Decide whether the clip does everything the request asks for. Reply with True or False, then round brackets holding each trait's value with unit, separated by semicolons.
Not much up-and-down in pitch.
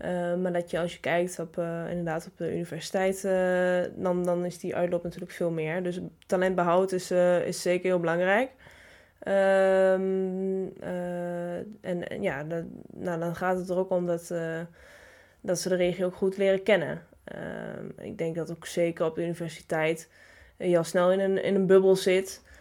True (1.7 semitones)